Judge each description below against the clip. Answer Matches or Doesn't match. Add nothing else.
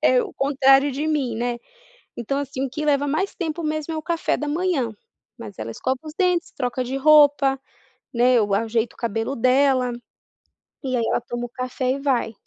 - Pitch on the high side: Matches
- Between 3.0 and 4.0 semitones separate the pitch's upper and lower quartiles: Matches